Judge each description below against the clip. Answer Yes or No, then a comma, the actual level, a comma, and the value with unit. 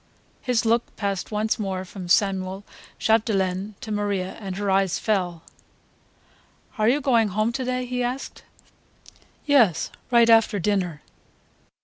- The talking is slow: Yes, slow, 130 wpm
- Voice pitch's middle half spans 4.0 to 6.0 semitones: No, average, 3.5 semitones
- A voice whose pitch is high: Yes, high, 210 Hz